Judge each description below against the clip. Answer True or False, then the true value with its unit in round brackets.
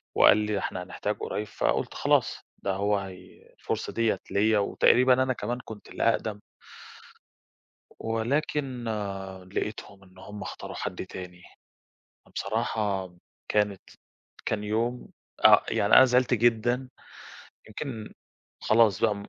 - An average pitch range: True (3.0 semitones)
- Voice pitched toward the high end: False (105 Hz)